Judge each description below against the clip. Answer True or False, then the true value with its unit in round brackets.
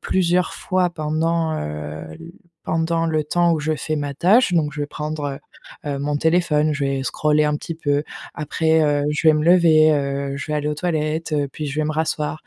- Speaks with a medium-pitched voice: True (155 Hz)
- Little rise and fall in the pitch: True (2.0 semitones)